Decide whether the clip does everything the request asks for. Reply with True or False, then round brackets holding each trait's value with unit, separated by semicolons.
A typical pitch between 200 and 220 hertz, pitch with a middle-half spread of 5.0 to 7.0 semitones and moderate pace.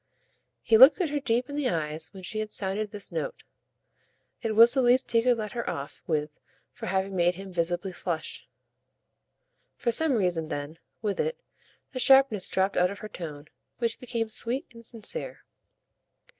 True (215 Hz; 5.5 semitones; 175 wpm)